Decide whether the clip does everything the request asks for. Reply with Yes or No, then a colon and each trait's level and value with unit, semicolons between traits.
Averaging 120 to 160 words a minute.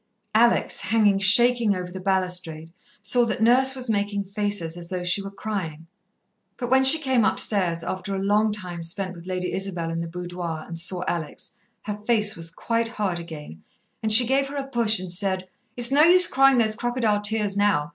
No: average, 195 wpm